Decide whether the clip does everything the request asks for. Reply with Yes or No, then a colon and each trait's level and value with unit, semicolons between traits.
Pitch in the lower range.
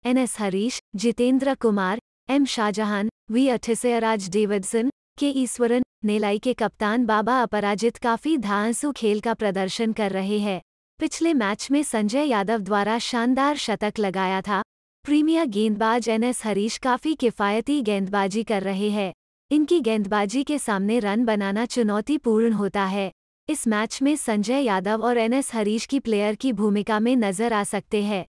No: high, 225 Hz